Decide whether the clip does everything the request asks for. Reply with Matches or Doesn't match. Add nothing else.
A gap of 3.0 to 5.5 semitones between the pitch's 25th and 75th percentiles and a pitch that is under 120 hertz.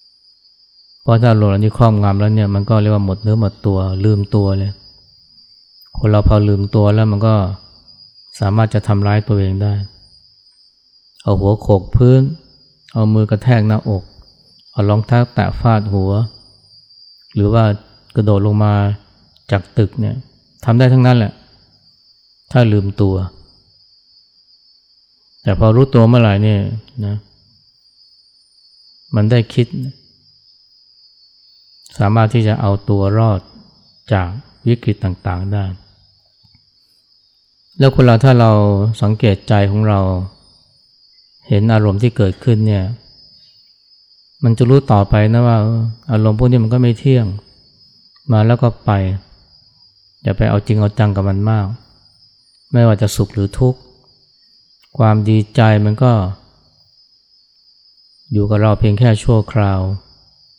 Doesn't match